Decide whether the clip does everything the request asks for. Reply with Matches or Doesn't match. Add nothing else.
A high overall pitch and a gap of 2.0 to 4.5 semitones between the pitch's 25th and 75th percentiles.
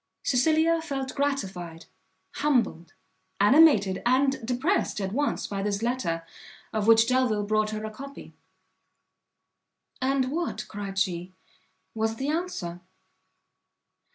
Doesn't match